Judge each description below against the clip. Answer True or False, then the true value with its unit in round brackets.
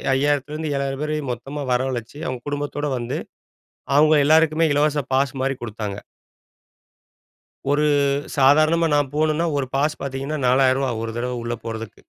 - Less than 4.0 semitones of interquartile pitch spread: True (2.7 semitones)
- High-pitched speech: False (140 Hz)